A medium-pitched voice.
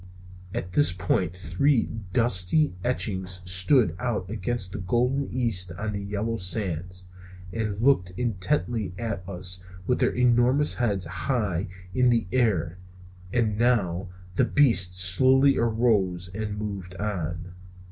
No: low, 100 Hz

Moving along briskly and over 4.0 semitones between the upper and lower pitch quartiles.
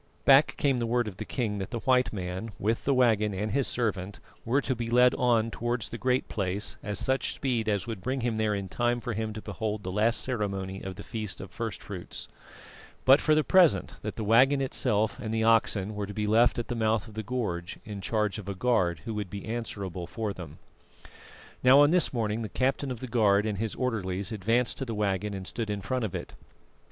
No: fast, 230 wpm; average, 3.3 semitones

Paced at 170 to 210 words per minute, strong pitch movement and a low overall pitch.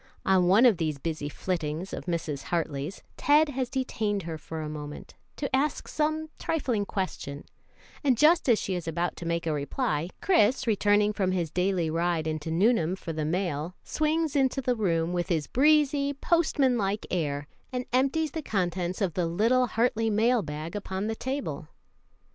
No: average, 175 wpm; wide, 7.5 semitones; high, 190 Hz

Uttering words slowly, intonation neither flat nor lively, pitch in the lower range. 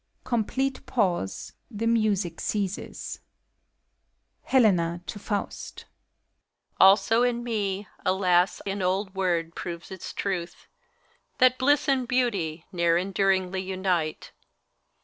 No: slow, 105 wpm; average, 4.1 semitones; high, 195 Hz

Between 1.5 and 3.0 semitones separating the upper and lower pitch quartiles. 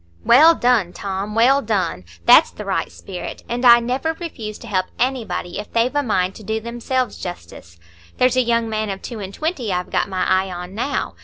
No: average, 4.7 semitones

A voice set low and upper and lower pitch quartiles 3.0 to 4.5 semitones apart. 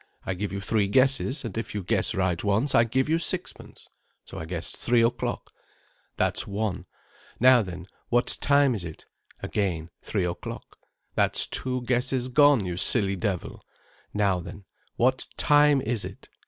No: low, 110 Hz; average, 5.2 semitones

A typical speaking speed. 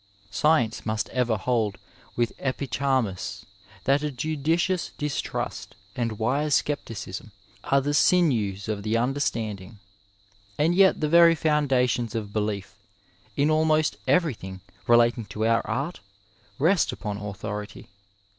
No: slow, 120 wpm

